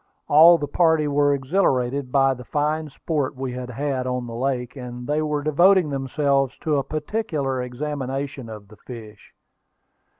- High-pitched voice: No, medium, 140 Hz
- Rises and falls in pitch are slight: No, average, 3.0 semitones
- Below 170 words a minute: Yes, average, 160 wpm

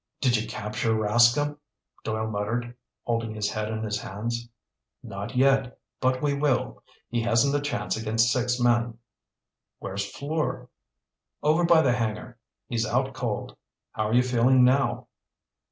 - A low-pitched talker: Yes, low, 120 Hz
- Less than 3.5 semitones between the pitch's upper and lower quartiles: Yes, average, 2.9 semitones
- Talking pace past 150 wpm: No, average, 145 wpm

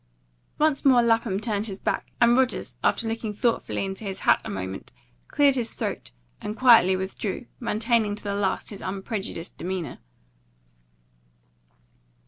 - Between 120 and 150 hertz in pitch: No, high, 210 Hz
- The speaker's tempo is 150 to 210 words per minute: No, average, 140 wpm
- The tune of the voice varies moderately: Yes, average, 3.6 semitones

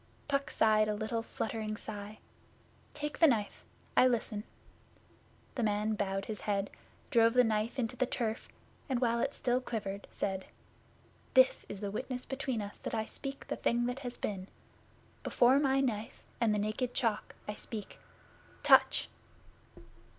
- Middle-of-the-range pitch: No, high, 225 Hz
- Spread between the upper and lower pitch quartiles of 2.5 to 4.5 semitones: Yes, average, 3.1 semitones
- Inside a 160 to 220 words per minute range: No, average, 150 wpm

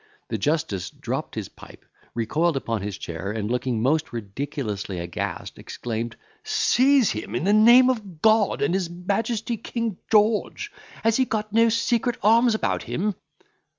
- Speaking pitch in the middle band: Yes, medium, 180 Hz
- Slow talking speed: No, average, 150 wpm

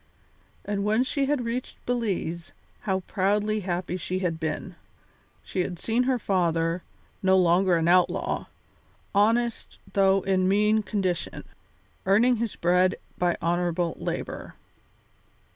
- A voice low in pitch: No, high, 190 Hz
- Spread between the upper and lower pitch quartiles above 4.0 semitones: No, average, 3.3 semitones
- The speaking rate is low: Yes, slow, 125 wpm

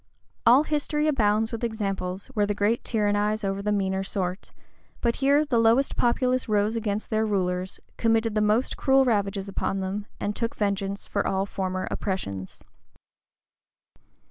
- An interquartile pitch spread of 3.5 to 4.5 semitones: No, average, 2.8 semitones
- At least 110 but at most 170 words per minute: Yes, average, 150 wpm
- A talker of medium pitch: No, high, 210 Hz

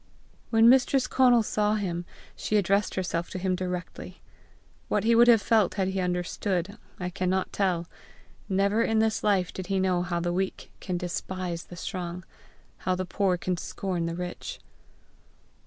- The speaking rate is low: No, average, 165 wpm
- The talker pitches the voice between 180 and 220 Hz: Yes, medium, 185 Hz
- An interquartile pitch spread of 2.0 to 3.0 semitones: Yes, average, 2.7 semitones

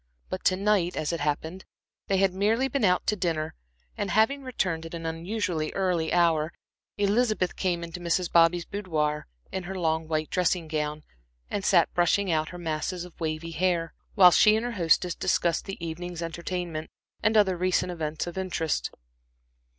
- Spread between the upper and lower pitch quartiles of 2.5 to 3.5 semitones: Yes, average, 2.8 semitones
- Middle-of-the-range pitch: Yes, medium, 175 Hz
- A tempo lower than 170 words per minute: No, average, 175 wpm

